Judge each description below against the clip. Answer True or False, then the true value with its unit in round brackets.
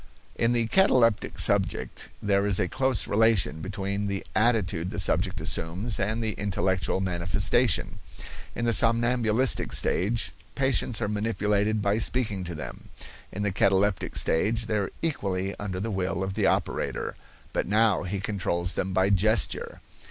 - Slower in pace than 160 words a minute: True (150 wpm)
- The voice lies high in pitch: False (105 Hz)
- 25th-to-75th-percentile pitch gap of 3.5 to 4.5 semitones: False (3.1 semitones)